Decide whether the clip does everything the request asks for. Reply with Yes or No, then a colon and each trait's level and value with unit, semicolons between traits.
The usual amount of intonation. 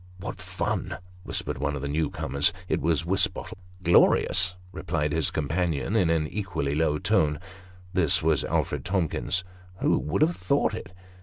Yes: average, 3.5 semitones